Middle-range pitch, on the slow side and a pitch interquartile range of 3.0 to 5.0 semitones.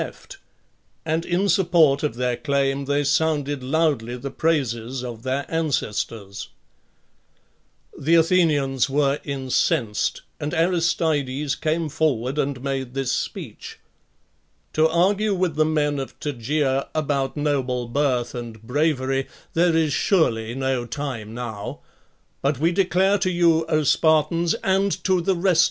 Yes: medium, 145 Hz; slow, 130 wpm; average, 3.8 semitones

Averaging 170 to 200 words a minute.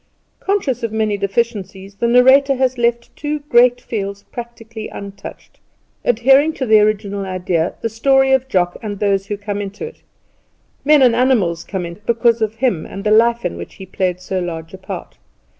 Yes: average, 180 wpm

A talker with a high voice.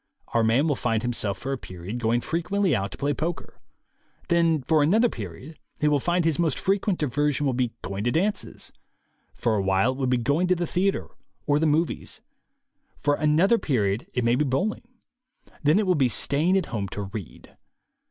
No: medium, 145 Hz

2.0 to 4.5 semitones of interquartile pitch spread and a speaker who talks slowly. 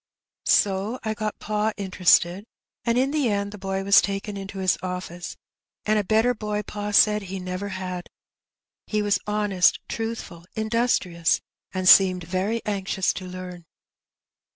No: narrow, 2.5 semitones; average, 150 wpm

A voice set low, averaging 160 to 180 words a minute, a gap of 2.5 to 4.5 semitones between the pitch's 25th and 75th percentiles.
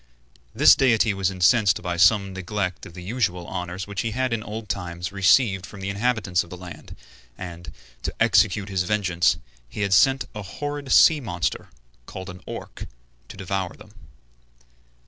Yes: very low, 95 Hz; average, 165 wpm; average, 3.4 semitones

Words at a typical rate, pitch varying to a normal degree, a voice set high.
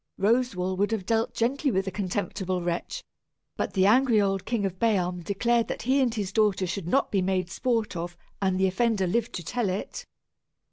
Yes: average, 195 wpm; average, 3.9 semitones; high, 200 Hz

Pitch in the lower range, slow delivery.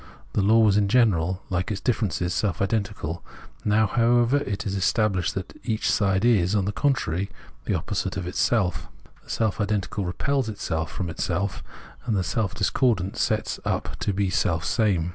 No: low, 100 Hz; average, 165 wpm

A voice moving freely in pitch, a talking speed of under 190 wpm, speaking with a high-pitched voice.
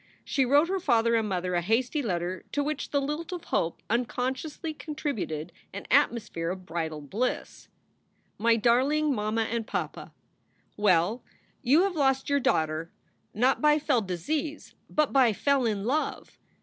Yes: wide, 7.0 semitones; average, 150 wpm; high, 240 Hz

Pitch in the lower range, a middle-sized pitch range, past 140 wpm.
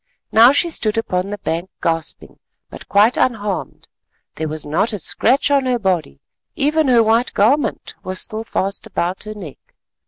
No: high, 210 Hz; average, 5.0 semitones; average, 165 wpm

